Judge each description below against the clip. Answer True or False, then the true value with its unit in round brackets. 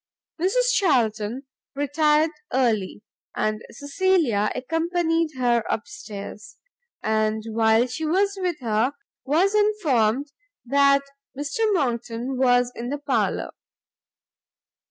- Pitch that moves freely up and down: True (6.1 semitones)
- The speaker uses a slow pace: True (100 wpm)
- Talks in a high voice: True (270 Hz)